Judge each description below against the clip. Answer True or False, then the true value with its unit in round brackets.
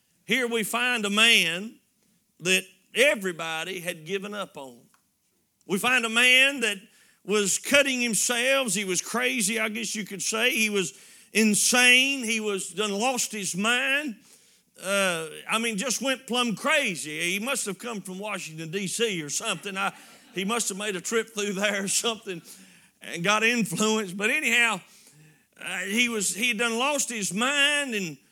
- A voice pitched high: True (215 Hz)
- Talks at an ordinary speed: True (165 wpm)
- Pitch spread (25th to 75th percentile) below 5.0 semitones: True (3.5 semitones)